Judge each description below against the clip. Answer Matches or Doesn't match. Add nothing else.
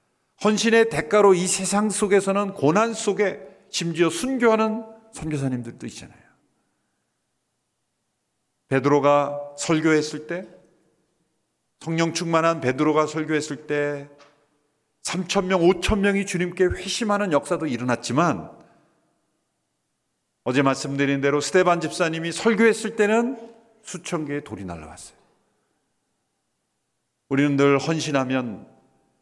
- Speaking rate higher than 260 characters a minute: Doesn't match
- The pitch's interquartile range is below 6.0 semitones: Matches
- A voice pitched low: Doesn't match